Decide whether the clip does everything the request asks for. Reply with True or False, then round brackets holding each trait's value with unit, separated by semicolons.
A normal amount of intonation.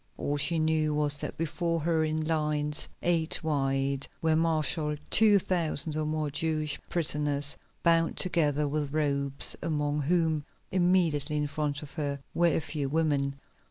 False (1.9 semitones)